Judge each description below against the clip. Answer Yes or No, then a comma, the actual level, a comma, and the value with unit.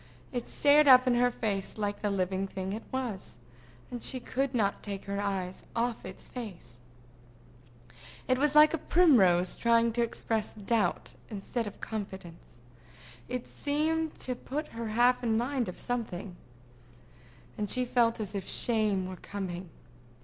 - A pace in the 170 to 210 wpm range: No, average, 155 wpm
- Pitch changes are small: No, average, 4.2 semitones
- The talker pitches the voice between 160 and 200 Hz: No, high, 225 Hz